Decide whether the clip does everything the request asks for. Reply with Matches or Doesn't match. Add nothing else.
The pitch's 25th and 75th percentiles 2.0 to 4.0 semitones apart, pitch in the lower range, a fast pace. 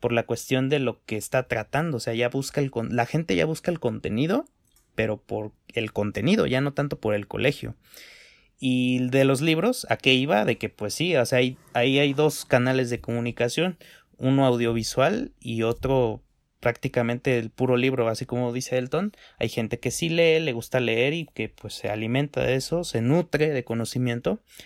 Matches